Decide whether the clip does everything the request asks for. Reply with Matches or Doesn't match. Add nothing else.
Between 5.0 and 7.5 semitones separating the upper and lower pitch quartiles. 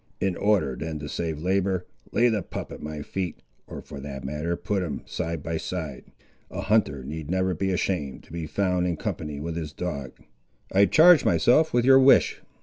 Doesn't match